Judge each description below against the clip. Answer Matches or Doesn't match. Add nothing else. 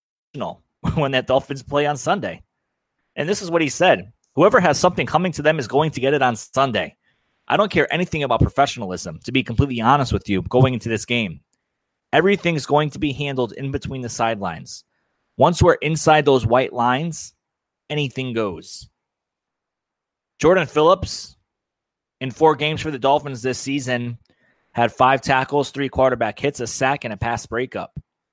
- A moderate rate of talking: Matches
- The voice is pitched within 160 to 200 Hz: Doesn't match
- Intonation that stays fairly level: Doesn't match